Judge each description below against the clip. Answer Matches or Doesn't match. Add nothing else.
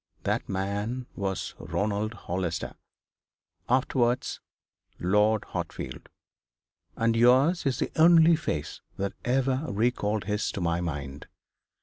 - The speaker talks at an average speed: Doesn't match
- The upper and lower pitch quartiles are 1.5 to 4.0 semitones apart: Doesn't match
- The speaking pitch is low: Matches